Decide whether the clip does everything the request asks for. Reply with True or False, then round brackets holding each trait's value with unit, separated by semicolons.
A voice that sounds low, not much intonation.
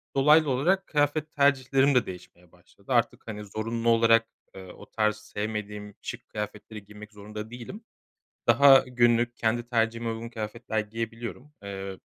False (115 Hz; 3.0 semitones)